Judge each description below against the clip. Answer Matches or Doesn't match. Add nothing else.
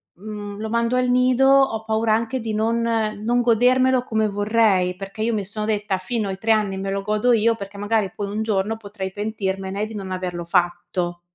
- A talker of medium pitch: Doesn't match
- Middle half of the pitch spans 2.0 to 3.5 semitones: Matches